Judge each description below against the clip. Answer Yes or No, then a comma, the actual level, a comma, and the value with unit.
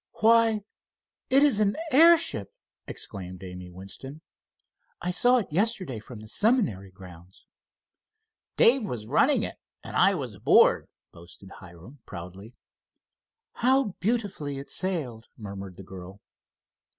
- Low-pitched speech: Yes, low, 125 Hz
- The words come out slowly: Yes, slow, 120 wpm